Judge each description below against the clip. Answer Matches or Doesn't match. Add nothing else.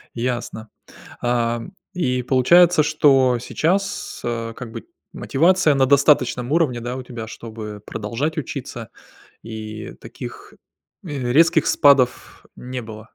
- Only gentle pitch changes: Doesn't match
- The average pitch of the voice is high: Doesn't match